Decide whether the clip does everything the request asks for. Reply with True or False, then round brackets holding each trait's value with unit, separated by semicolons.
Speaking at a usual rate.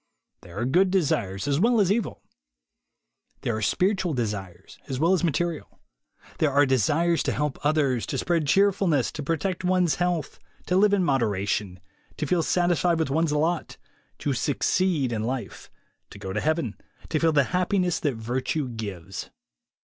True (170 wpm)